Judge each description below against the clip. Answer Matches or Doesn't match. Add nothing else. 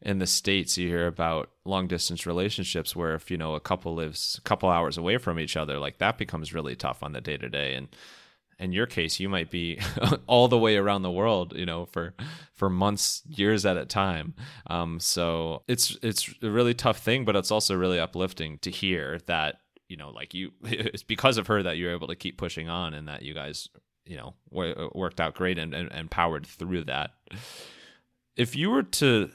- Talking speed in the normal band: Doesn't match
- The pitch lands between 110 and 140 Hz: Doesn't match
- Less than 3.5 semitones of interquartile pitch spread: Doesn't match